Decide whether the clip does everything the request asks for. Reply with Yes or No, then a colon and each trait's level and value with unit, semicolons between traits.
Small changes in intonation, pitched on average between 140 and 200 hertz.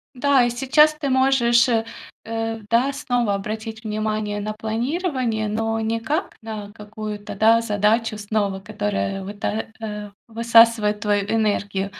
No: narrow, 2.0 semitones; high, 220 Hz